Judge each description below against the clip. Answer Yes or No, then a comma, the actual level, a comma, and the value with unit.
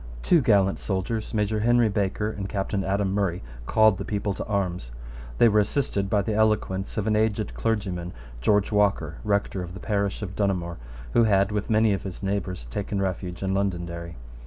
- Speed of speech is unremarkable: Yes, average, 185 wpm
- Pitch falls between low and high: No, low, 100 Hz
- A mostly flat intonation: Yes, narrow, 2.0 semitones